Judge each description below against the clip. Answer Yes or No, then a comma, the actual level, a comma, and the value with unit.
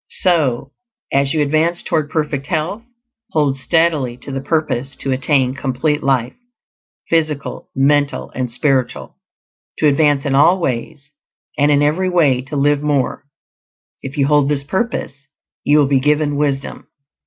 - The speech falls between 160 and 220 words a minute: No, average, 145 wpm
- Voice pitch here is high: No, medium, 145 Hz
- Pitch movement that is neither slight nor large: No, narrow, 2.2 semitones